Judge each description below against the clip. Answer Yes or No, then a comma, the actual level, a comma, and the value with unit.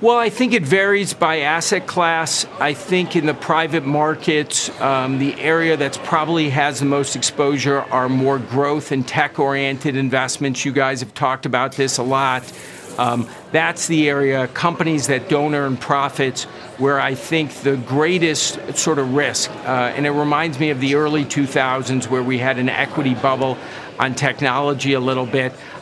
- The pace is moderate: Yes, average, 175 wpm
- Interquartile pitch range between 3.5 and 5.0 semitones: No, average, 2.8 semitones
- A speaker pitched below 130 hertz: No, medium, 140 Hz